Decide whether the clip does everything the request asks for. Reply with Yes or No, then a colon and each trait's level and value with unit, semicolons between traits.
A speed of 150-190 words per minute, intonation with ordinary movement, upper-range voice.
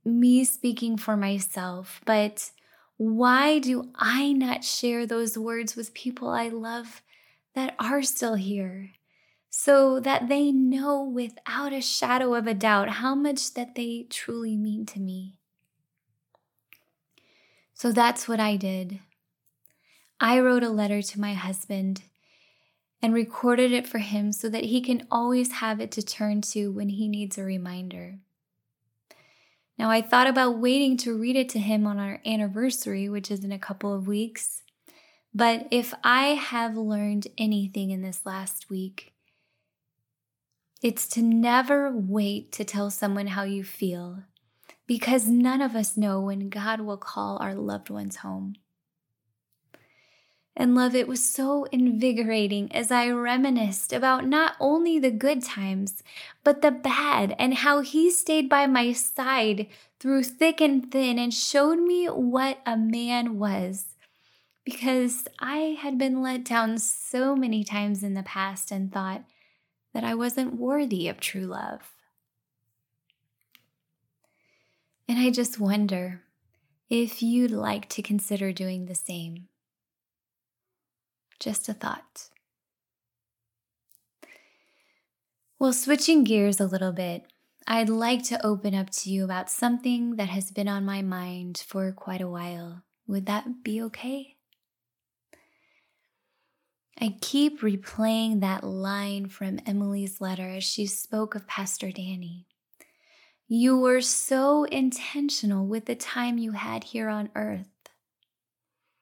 No: average, 140 wpm; average, 4.5 semitones; high, 220 Hz